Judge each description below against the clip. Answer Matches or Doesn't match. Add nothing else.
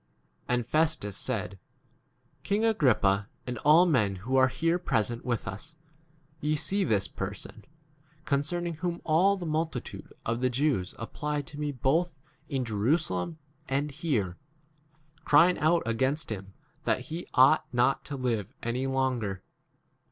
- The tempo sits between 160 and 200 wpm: Doesn't match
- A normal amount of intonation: Doesn't match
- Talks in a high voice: Doesn't match